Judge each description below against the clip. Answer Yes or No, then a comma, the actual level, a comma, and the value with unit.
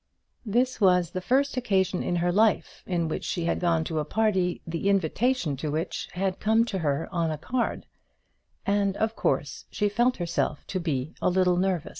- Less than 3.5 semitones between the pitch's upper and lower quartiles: No, average, 4.1 semitones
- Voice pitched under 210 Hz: Yes, medium, 185 Hz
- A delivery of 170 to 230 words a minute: Yes, average, 190 wpm